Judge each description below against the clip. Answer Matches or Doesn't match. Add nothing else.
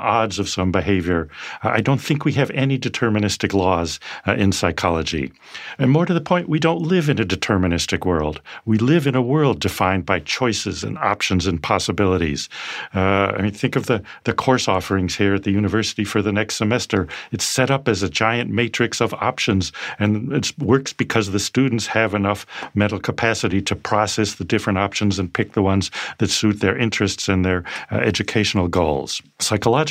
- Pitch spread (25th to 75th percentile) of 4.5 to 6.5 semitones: Doesn't match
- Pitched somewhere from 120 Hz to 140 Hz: Doesn't match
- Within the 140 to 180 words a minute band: Doesn't match